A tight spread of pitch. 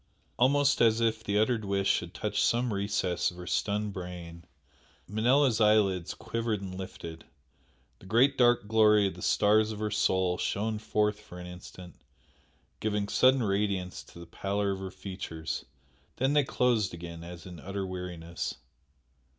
No: average, 3.4 semitones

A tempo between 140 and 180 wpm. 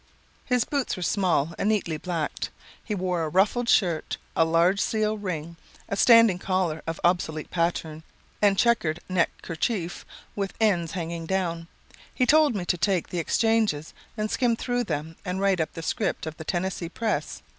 Yes: average, 170 wpm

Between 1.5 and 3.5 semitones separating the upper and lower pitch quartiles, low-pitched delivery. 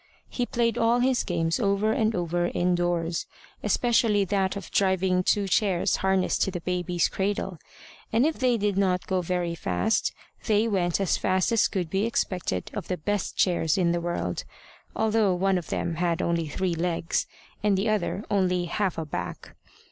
No: average, 2.9 semitones; medium, 185 Hz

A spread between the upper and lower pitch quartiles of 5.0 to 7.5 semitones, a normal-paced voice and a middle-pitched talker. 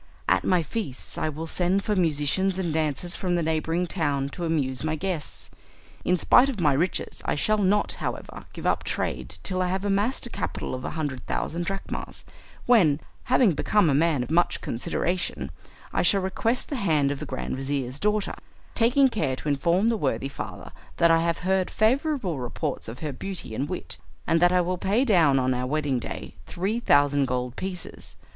Yes: average, 5.3 semitones; average, 195 wpm; medium, 170 Hz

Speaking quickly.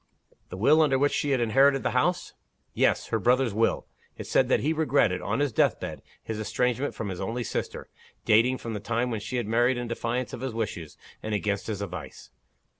Yes: fast, 210 wpm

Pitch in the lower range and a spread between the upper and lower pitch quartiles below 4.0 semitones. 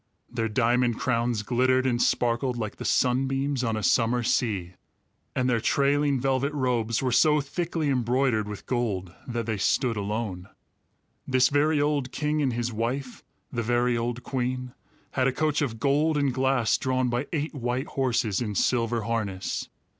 Yes: low, 125 Hz; narrow, 2.6 semitones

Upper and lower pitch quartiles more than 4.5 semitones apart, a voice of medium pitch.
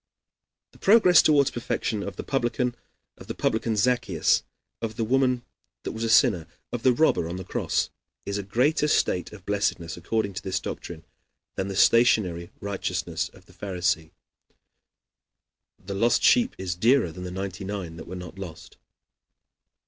No: average, 4.9 semitones; low, 100 Hz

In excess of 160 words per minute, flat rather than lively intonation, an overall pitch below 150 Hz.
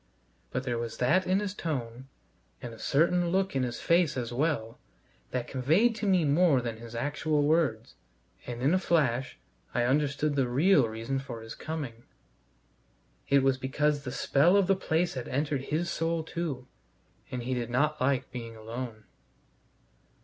No: average, 170 wpm; average, 4.9 semitones; medium, 140 Hz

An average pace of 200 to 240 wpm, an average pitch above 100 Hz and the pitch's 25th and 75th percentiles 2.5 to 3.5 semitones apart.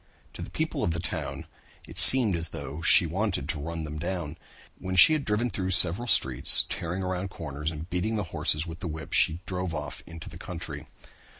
No: fast, 205 wpm; very low, 85 Hz; average, 2.9 semitones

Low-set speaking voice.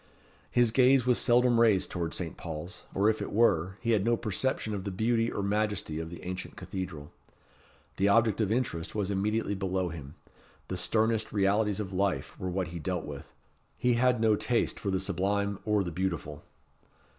Yes: low, 100 Hz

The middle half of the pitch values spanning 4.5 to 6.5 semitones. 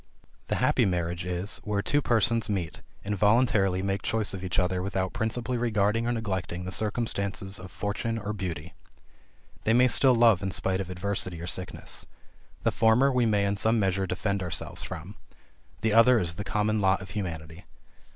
No: average, 3.3 semitones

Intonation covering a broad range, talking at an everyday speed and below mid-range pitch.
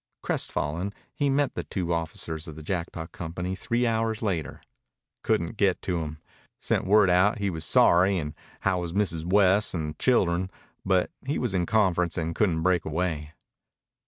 No: average, 3.6 semitones; average, 170 wpm; very low, 90 Hz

